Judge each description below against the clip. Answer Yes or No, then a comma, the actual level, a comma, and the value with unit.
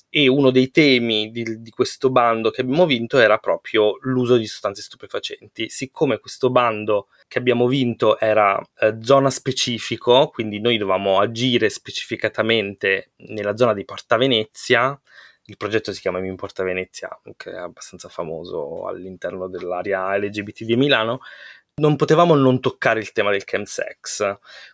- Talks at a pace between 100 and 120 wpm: No, average, 150 wpm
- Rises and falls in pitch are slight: No, average, 3.7 semitones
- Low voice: Yes, low, 115 Hz